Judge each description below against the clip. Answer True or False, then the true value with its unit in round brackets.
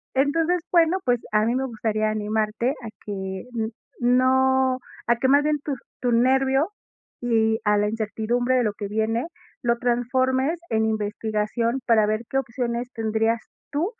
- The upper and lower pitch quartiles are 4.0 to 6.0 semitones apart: False (3.1 semitones)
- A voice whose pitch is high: True (235 Hz)